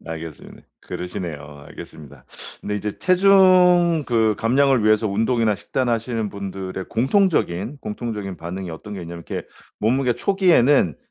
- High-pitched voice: No, low, 110 Hz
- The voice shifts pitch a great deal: Yes, wide, 6.5 semitones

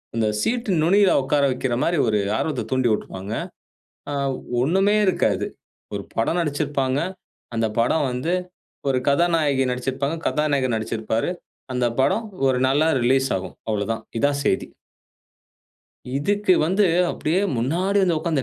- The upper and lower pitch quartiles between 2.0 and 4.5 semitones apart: No, average, 5.2 semitones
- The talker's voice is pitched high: No, medium, 140 Hz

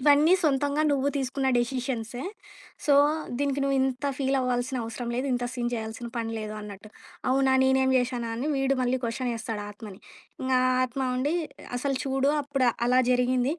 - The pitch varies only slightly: Yes, narrow, 2.2 semitones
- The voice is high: Yes, very high, 255 Hz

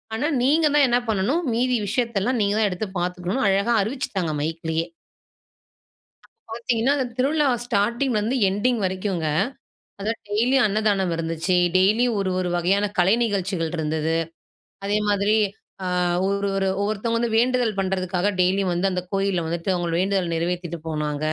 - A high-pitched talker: Yes, high, 200 Hz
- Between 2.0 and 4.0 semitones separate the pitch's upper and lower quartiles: No, average, 4.4 semitones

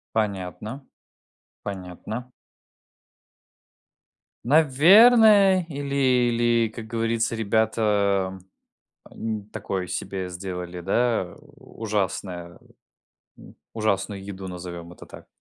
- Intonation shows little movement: No, average, 4.2 semitones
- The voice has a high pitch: No, low, 105 Hz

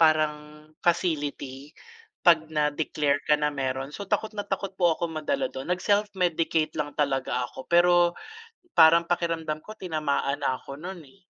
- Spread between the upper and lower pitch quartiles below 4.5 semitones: Yes, average, 3.1 semitones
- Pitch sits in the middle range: Yes, medium, 155 Hz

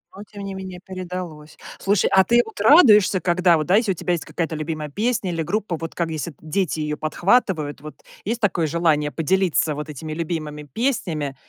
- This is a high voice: No, medium, 170 Hz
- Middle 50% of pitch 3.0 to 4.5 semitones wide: Yes, average, 4.0 semitones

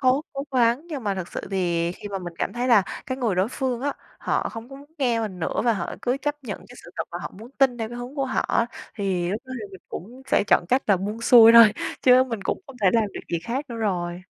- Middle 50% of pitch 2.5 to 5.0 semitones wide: Yes, average, 4.7 semitones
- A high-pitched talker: Yes, high, 230 Hz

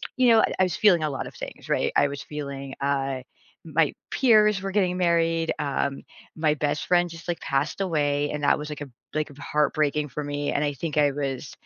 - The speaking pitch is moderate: Yes, medium, 150 Hz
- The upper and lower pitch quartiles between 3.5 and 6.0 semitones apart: No, average, 3.1 semitones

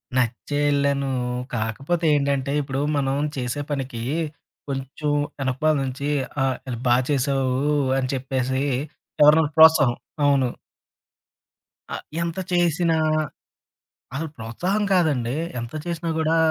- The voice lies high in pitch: No, medium, 140 Hz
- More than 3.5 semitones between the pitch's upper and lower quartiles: No, average, 3.2 semitones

